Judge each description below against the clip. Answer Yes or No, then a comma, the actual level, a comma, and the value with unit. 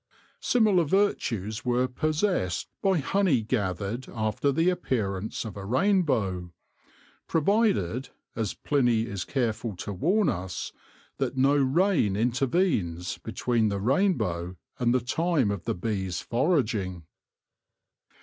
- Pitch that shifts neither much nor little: No, wide, 7.8 semitones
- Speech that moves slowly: Yes, slow, 120 wpm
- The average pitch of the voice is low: Yes, low, 120 Hz